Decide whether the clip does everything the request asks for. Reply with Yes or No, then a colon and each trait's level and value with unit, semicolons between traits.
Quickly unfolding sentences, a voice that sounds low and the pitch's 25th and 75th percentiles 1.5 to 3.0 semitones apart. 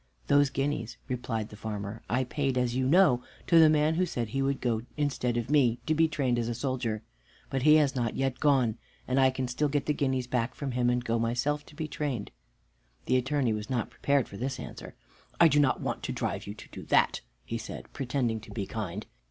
No: fast, 225 wpm; low, 130 Hz; average, 3.5 semitones